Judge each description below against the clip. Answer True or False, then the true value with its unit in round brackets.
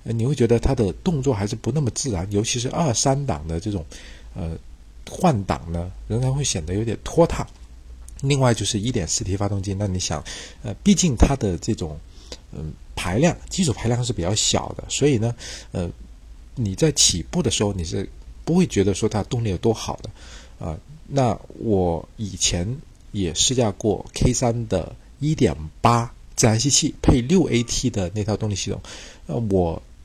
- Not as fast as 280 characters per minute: True (260 characters per minute)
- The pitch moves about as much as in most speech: False (6.2 semitones)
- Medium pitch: False (105 Hz)